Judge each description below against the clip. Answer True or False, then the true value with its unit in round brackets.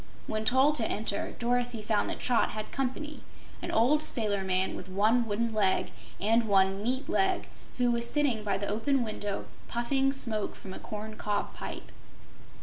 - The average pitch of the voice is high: True (225 Hz)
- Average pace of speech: True (170 wpm)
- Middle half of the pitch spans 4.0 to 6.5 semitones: False (3.3 semitones)